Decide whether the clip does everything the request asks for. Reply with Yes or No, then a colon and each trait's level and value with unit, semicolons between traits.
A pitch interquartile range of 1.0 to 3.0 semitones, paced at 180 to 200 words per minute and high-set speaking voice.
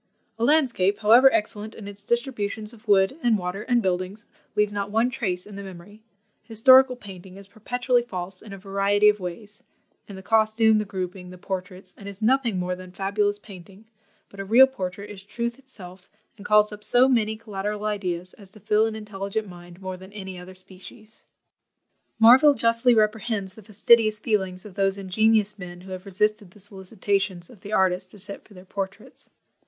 Yes: narrow, 2.6 semitones; average, 185 wpm; high, 205 Hz